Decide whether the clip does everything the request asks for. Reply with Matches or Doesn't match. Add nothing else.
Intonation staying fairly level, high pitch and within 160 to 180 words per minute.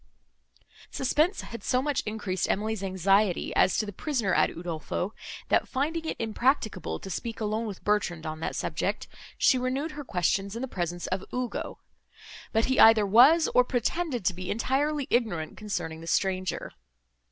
Doesn't match